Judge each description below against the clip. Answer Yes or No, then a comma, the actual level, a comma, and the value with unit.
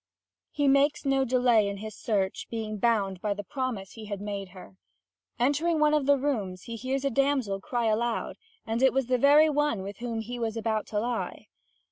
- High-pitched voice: Yes, high, 235 Hz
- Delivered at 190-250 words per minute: Yes, average, 200 wpm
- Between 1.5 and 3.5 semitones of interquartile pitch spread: No, average, 4.6 semitones